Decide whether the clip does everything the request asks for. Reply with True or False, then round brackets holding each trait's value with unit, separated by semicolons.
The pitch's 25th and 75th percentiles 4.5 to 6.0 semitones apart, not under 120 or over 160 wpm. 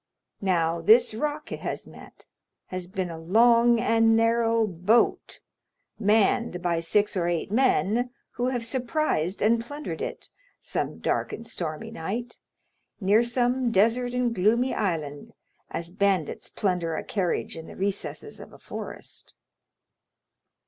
True (4.9 semitones; 135 wpm)